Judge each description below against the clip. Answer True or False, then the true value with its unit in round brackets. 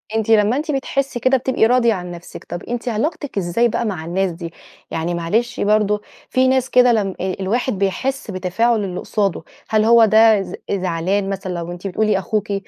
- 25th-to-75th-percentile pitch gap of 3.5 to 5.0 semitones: True (4.3 semitones)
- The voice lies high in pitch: True (210 Hz)